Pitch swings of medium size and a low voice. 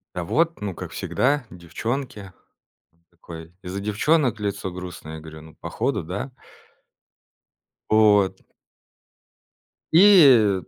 No: wide, 6.5 semitones; low, 100 Hz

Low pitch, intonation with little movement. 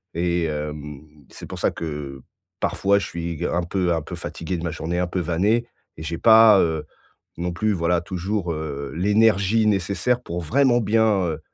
No: very low, 85 Hz; average, 4.1 semitones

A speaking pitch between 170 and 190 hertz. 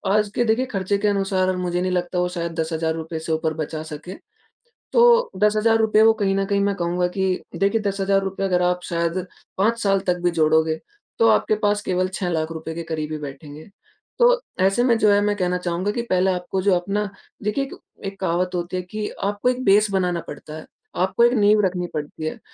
Yes: medium, 185 Hz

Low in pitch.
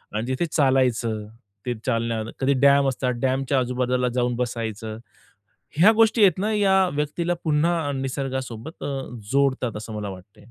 Yes: low, 130 Hz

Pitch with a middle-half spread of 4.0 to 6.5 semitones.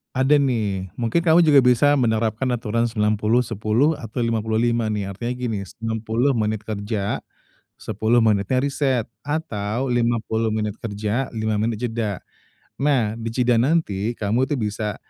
No: average, 2.7 semitones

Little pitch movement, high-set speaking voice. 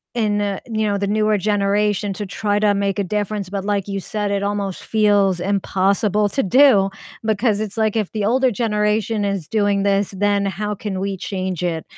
Yes: narrow, 1.2 semitones; high, 205 Hz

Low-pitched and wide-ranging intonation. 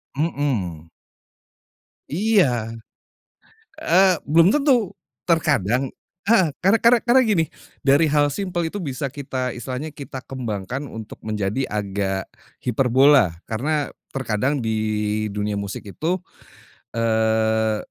Yes: low, 130 Hz; wide, 6.7 semitones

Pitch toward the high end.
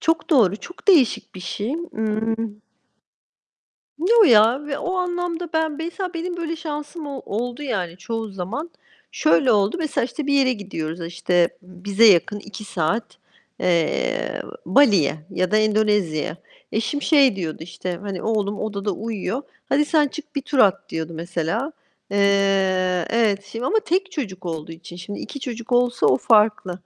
Yes: high, 220 Hz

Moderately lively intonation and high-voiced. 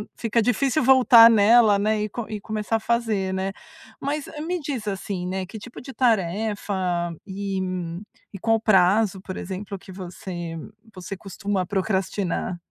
Yes: average, 3.2 semitones; high, 205 Hz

